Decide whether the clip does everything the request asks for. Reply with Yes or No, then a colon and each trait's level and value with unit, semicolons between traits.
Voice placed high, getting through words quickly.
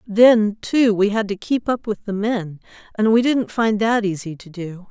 Yes: high, 210 Hz; fast, 220 wpm